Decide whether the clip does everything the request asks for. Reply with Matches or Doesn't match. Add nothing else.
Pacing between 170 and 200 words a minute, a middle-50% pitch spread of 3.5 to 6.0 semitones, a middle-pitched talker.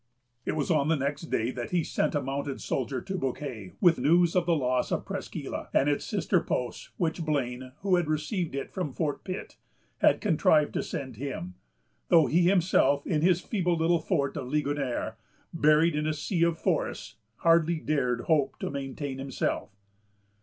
Matches